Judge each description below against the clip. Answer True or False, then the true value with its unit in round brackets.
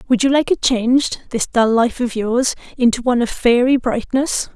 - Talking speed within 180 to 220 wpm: False (170 wpm)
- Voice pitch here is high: True (245 Hz)